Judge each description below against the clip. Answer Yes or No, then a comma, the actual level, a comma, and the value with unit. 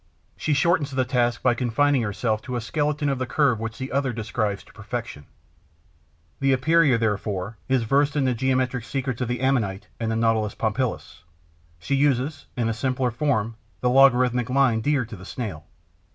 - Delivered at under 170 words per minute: No, average, 180 wpm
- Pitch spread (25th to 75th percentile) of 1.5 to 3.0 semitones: No, average, 3.4 semitones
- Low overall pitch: Yes, low, 125 Hz